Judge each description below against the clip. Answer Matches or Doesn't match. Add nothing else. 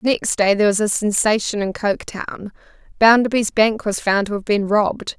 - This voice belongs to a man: Doesn't match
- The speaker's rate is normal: Matches